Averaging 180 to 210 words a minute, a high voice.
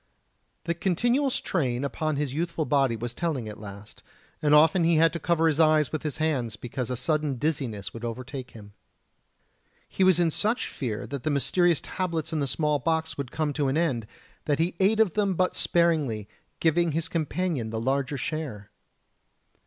No: average, 185 wpm; medium, 150 Hz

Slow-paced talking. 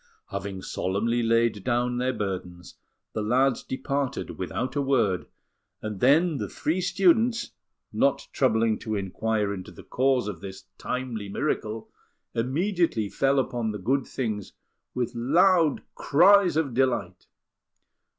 Yes: slow, 130 wpm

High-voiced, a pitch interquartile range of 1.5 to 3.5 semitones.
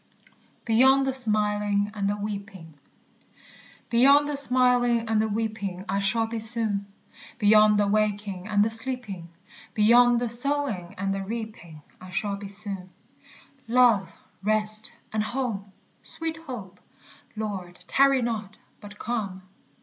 Yes: high, 215 Hz; average, 3.1 semitones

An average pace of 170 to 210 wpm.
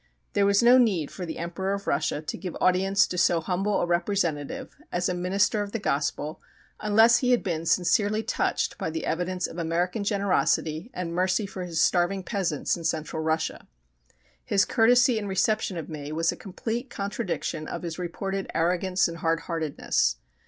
Yes: average, 180 wpm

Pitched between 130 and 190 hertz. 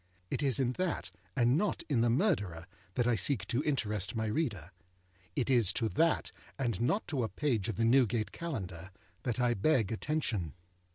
No: low, 120 Hz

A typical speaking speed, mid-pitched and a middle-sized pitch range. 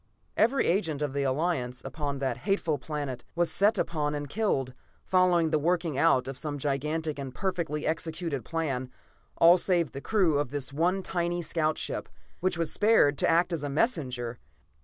Yes: average, 175 wpm; medium, 155 Hz; average, 3.8 semitones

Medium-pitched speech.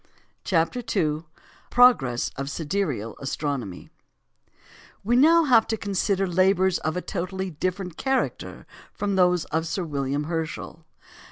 Yes: medium, 180 Hz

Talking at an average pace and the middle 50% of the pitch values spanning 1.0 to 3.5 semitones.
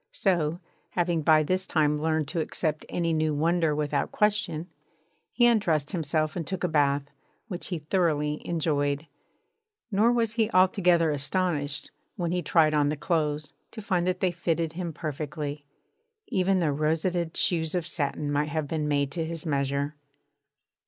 Yes: average, 160 wpm; average, 3.1 semitones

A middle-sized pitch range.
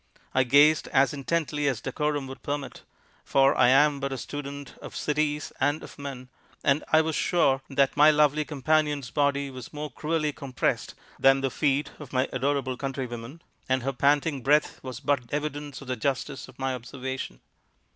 No: narrow, 2.0 semitones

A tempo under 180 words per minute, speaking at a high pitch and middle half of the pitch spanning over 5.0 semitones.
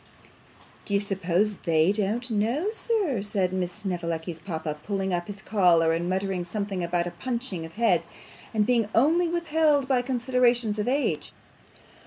Yes: average, 155 wpm; high, 205 Hz; wide, 5.6 semitones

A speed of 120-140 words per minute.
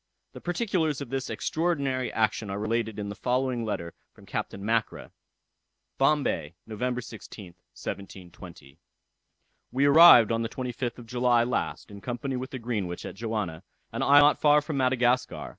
No: average, 155 wpm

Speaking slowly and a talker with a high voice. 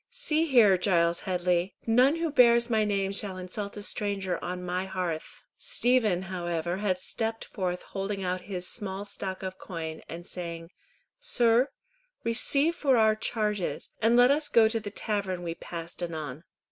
No: average, 160 wpm; high, 195 Hz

